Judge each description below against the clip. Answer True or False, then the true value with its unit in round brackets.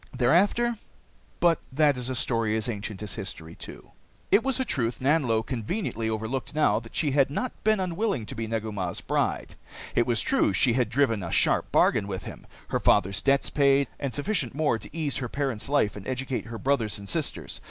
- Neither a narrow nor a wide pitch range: True (4.8 semitones)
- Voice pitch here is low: True (125 Hz)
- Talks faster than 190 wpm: True (200 wpm)